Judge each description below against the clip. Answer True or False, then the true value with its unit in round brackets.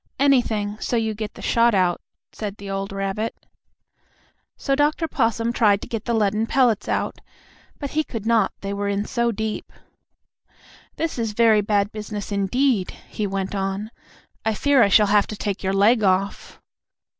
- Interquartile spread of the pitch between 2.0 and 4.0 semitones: True (2.7 semitones)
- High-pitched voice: True (215 Hz)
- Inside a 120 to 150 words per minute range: False (170 wpm)